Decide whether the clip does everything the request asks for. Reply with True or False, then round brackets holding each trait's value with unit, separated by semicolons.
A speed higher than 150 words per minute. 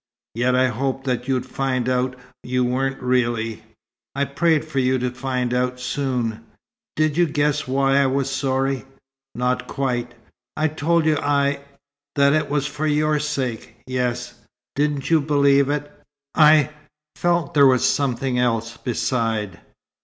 False (145 wpm)